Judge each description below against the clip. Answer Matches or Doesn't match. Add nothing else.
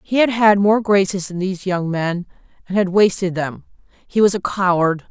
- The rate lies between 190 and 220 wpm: Matches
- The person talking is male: Doesn't match